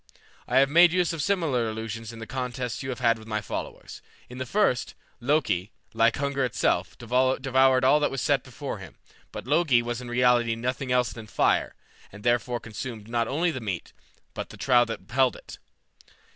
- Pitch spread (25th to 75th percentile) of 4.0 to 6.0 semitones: No, average, 2.8 semitones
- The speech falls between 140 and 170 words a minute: No, average, 190 wpm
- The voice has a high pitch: No, low, 125 Hz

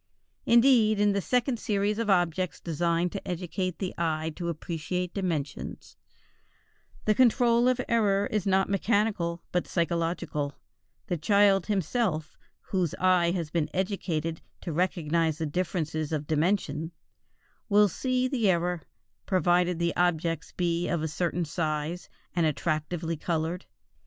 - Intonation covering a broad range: No, average, 3.5 semitones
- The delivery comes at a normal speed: No, slow, 130 wpm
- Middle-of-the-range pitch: Yes, medium, 175 Hz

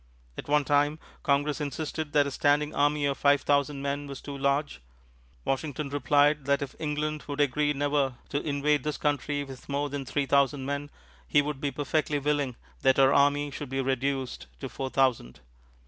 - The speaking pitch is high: No, medium, 145 Hz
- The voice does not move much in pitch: Yes, narrow, 1.1 semitones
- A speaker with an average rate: Yes, average, 180 wpm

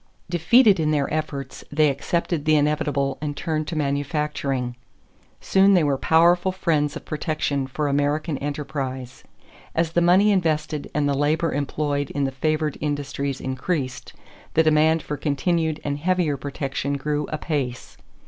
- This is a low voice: No, medium, 150 Hz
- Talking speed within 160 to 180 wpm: No, average, 145 wpm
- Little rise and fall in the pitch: Yes, narrow, 2.2 semitones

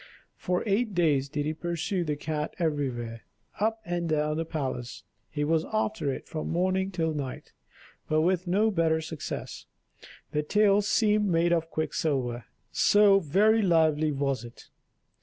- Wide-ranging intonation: No, average, 4.2 semitones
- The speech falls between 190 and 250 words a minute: No, average, 150 wpm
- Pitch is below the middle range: No, medium, 160 Hz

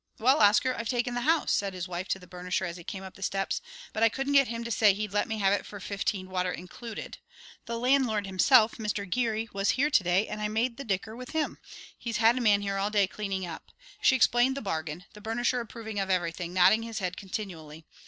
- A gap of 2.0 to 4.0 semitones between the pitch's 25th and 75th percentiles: Yes, average, 3.7 semitones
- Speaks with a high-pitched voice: Yes, high, 210 Hz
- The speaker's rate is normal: No, fast, 240 wpm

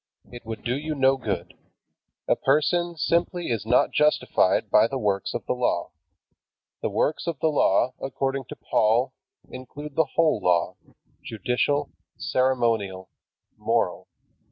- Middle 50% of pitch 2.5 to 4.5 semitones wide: No, average, 5.0 semitones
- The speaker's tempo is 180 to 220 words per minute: No, slow, 135 wpm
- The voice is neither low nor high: No, low, 130 Hz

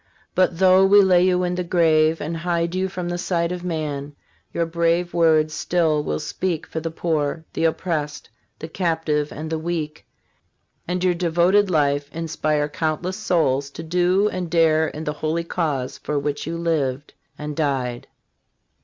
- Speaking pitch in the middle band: Yes, medium, 165 Hz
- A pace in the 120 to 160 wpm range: No, average, 170 wpm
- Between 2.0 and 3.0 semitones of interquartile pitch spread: Yes, average, 2.7 semitones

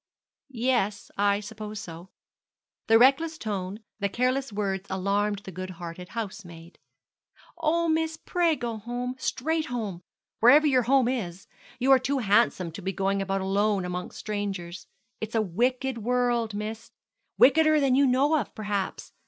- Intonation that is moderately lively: Yes, average, 4.9 semitones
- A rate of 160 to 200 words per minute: No, average, 150 wpm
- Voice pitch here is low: No, high, 220 Hz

